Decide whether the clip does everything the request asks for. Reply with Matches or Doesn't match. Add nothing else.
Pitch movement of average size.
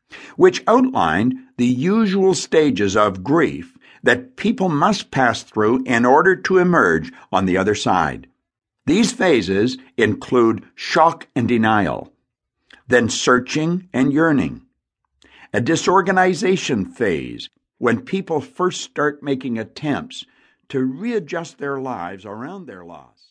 Doesn't match